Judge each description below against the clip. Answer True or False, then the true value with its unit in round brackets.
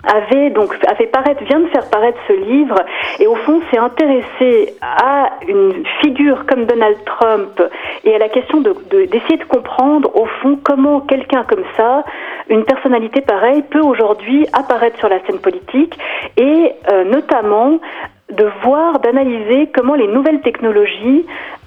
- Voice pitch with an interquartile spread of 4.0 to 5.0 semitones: True (4.7 semitones)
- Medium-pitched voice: False (275 Hz)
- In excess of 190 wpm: False (155 wpm)